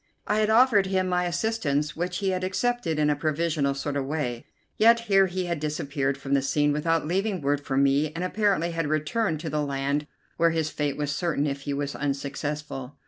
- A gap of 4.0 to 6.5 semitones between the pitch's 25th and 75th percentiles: Yes, average, 4.3 semitones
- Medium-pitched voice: Yes, medium, 155 Hz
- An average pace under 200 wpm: No, fast, 205 wpm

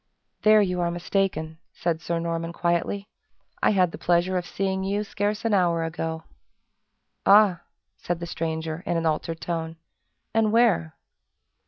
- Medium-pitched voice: Yes, medium, 175 Hz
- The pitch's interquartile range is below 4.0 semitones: Yes, average, 3.0 semitones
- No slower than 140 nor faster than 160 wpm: Yes, average, 150 wpm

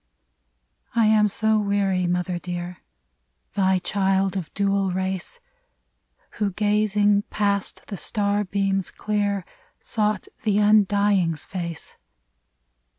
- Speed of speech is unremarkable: No, slow, 105 wpm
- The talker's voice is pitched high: Yes, high, 200 Hz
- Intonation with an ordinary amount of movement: No, narrow, 2.0 semitones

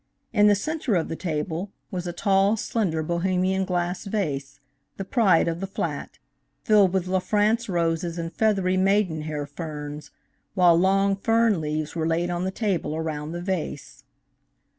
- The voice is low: No, medium, 180 Hz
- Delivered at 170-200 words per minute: No, average, 160 wpm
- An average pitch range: Yes, average, 3.4 semitones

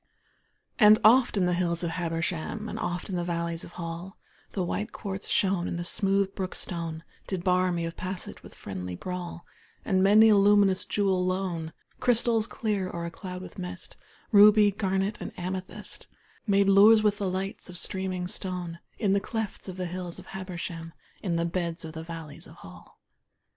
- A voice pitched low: No, medium, 185 Hz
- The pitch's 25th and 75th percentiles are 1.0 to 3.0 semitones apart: Yes, narrow, 2.6 semitones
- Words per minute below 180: No, average, 185 wpm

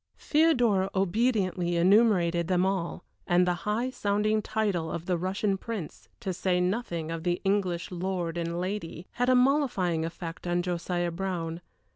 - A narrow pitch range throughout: No, average, 3.3 semitones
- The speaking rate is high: No, average, 150 wpm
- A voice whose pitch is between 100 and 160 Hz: No, medium, 185 Hz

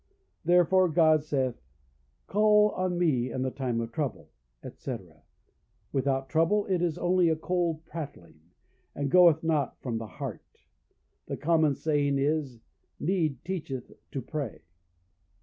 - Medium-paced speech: No, slow, 130 wpm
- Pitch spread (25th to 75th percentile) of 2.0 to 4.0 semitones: No, average, 4.6 semitones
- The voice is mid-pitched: Yes, medium, 155 Hz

